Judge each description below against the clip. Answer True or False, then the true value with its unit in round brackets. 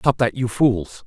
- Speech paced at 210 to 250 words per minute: True (225 wpm)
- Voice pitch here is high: False (115 Hz)